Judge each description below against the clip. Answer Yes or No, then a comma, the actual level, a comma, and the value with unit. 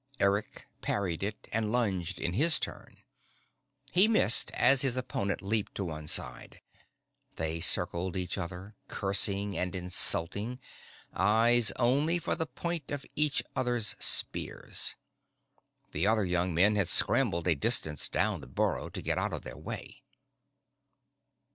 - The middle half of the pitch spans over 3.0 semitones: Yes, wide, 5.4 semitones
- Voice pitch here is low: Yes, low, 100 Hz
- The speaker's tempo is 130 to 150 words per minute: Yes, average, 140 wpm